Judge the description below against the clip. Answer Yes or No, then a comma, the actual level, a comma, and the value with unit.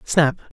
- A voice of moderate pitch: Yes, medium, 150 Hz